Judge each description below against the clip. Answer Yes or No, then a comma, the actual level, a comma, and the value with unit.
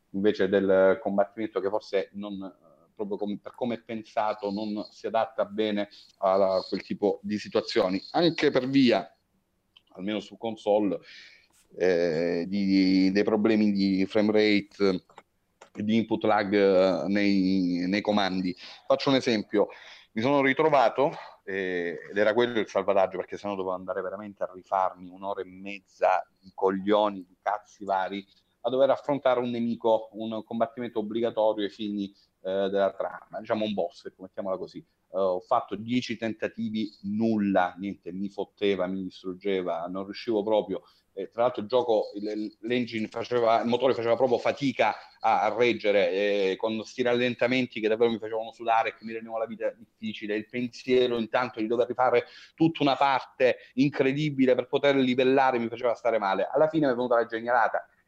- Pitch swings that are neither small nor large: Yes, average, 3.6 semitones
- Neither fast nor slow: Yes, average, 160 wpm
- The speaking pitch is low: Yes, low, 105 Hz